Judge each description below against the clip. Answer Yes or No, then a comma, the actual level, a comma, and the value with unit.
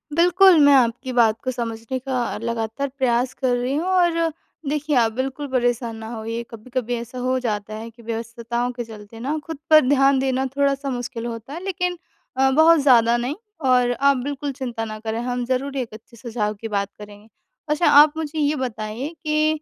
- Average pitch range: Yes, average, 3.6 semitones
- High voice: Yes, very high, 250 Hz